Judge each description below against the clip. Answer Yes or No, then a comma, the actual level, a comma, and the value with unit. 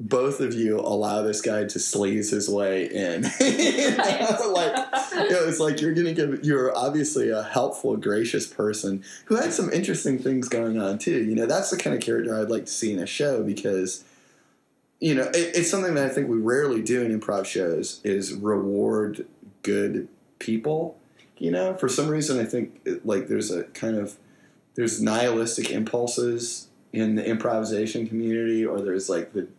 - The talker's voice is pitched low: Yes, low, 115 Hz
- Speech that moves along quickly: No, average, 185 wpm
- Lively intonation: Yes, wide, 5.7 semitones